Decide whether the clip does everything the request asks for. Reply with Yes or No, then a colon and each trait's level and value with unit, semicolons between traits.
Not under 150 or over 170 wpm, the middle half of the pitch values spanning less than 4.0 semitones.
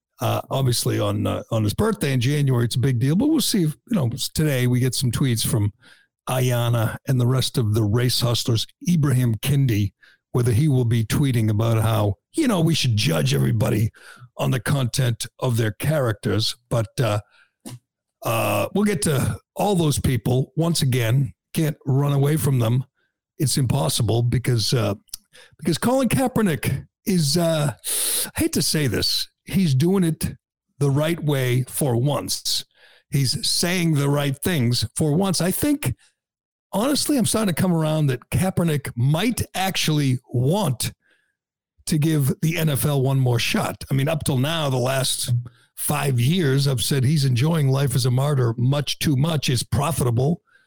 No: average, 165 wpm; average, 4.3 semitones